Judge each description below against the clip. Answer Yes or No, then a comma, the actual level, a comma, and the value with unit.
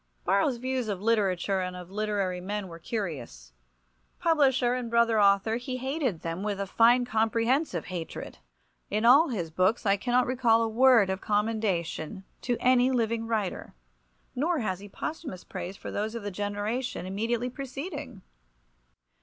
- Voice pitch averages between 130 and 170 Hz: No, high, 220 Hz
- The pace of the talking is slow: No, average, 155 wpm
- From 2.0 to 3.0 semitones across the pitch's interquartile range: No, average, 4.2 semitones